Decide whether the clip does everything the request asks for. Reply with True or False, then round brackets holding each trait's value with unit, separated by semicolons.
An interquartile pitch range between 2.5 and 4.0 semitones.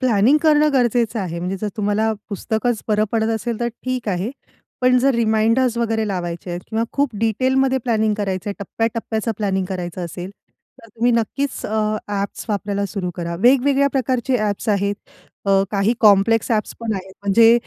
True (3.2 semitones)